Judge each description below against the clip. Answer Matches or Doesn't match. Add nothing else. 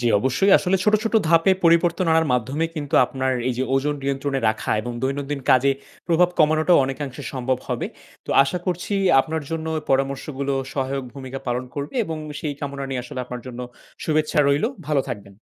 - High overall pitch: Doesn't match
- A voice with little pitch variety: Doesn't match